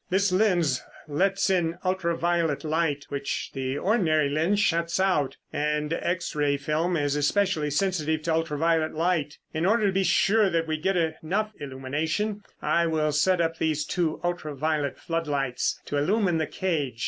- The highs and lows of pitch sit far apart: No, average, 3.6 semitones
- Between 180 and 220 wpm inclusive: No, average, 165 wpm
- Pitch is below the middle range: No, medium, 165 Hz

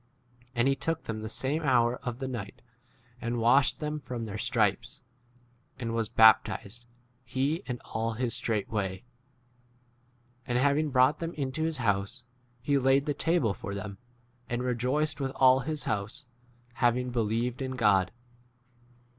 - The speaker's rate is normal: Yes, average, 155 wpm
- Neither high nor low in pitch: No, low, 125 Hz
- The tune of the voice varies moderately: Yes, average, 3.3 semitones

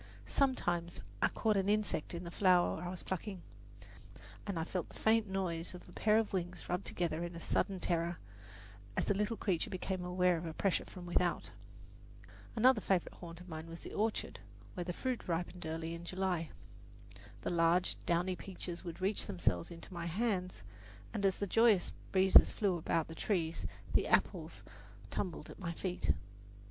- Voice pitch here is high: No, medium, 180 Hz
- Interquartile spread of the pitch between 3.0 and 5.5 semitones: No, narrow, 2.4 semitones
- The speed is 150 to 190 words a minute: Yes, average, 180 wpm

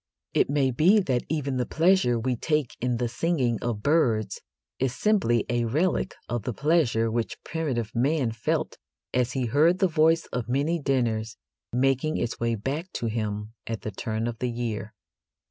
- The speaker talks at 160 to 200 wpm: Yes, average, 175 wpm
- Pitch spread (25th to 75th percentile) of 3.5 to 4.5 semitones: No, average, 5.0 semitones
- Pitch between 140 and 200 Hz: No, low, 125 Hz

